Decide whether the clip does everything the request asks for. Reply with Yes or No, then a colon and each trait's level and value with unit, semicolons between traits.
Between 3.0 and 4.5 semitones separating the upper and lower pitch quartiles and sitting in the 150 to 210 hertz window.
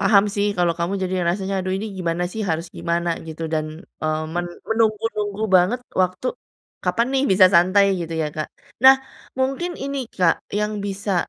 Yes: average, 3.8 semitones; high, 190 Hz